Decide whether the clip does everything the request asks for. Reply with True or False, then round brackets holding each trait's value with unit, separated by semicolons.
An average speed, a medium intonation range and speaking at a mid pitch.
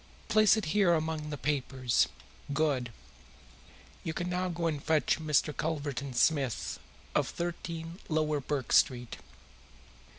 False (125 wpm; 3.1 semitones; 155 Hz)